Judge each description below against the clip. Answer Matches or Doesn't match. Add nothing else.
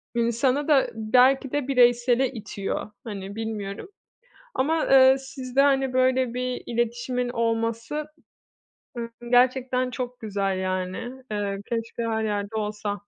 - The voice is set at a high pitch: Matches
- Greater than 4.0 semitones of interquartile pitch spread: Doesn't match